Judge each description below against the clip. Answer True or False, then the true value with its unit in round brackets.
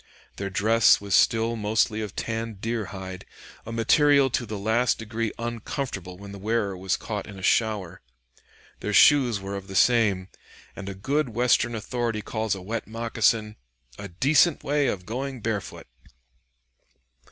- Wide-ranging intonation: False (3.0 semitones)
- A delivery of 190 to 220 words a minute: False (155 wpm)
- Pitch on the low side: True (110 Hz)